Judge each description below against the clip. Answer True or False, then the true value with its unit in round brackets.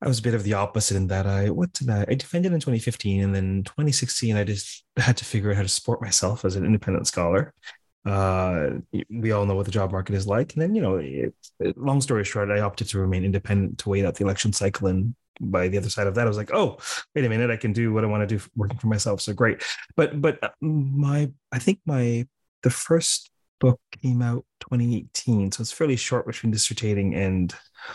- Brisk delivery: True (235 wpm)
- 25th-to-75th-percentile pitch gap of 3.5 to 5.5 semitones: True (4.0 semitones)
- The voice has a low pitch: True (110 Hz)